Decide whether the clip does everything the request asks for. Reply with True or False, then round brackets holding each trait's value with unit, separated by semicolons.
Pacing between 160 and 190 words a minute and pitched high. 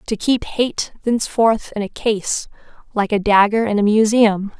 True (170 wpm; 215 Hz)